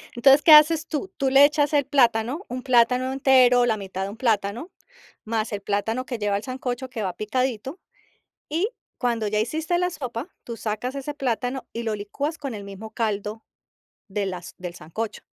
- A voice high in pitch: Yes, high, 245 Hz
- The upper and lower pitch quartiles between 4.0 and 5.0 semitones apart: Yes, average, 4.3 semitones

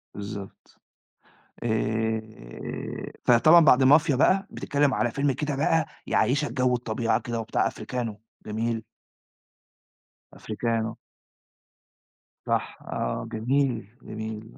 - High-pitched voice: No, low, 120 Hz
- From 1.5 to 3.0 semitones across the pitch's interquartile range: No, average, 4.0 semitones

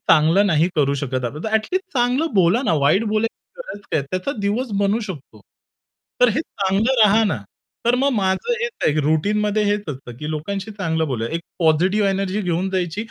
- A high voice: Yes, high, 195 Hz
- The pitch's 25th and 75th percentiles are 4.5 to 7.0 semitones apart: Yes, average, 5.3 semitones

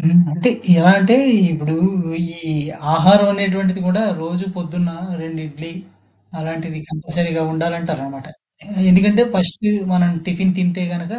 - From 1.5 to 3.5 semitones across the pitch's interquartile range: Yes, narrow, 2.5 semitones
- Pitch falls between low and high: Yes, medium, 175 Hz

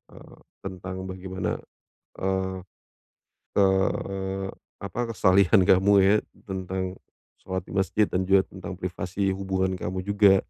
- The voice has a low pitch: Yes, very low, 95 Hz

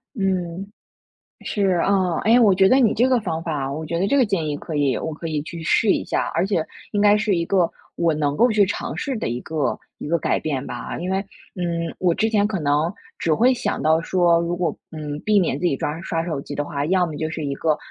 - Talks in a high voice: No, medium, 170 Hz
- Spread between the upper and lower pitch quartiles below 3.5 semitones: No, average, 4.2 semitones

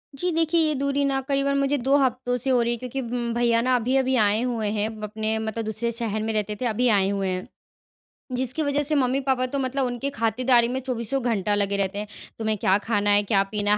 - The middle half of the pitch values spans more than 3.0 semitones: Yes, average, 3.8 semitones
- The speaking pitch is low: No, high, 240 Hz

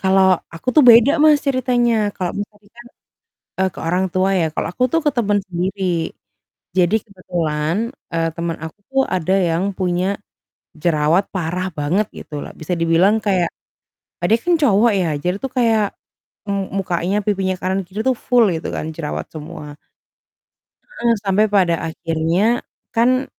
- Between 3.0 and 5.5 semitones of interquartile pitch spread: Yes, average, 4.9 semitones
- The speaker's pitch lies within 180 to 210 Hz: Yes, high, 190 Hz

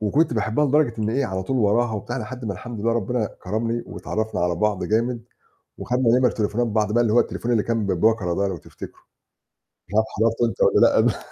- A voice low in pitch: Yes, low, 110 Hz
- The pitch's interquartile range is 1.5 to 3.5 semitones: Yes, narrow, 2.4 semitones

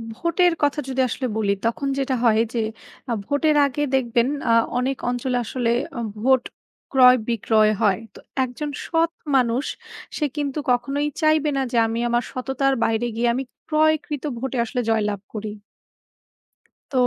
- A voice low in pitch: No, very high, 255 Hz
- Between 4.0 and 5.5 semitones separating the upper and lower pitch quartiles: No, average, 3.5 semitones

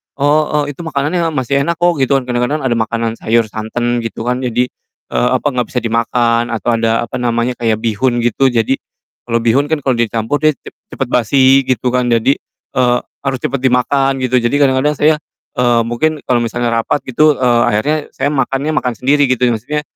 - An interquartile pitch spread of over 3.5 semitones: No, average, 2.9 semitones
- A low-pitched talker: Yes, low, 125 Hz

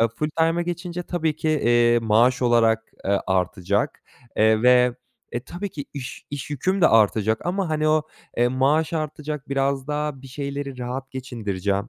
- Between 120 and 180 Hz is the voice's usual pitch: Yes, low, 135 Hz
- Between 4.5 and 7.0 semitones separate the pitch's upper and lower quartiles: Yes, average, 4.8 semitones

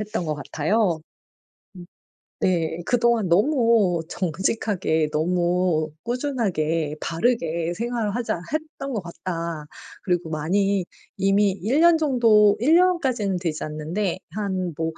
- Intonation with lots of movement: Yes, wide, 5.7 semitones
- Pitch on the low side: No, high, 190 Hz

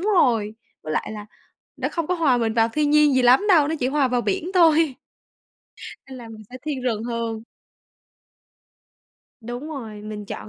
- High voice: Yes, very high, 250 Hz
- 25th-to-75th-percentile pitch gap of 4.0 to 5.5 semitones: Yes, average, 5.2 semitones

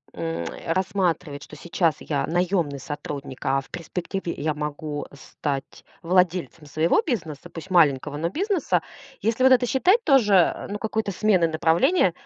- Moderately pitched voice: Yes, medium, 170 Hz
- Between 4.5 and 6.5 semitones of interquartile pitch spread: Yes, average, 5.3 semitones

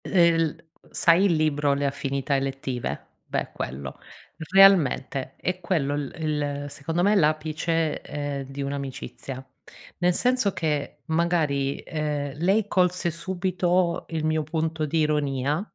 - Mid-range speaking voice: Yes, medium, 155 Hz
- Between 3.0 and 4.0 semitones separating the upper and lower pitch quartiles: Yes, average, 3.5 semitones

